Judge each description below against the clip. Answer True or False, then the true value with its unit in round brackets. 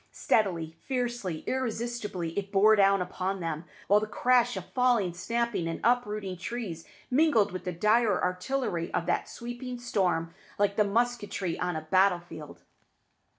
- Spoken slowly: False (150 wpm)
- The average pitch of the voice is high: True (200 Hz)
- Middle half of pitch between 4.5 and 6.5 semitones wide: True (5.1 semitones)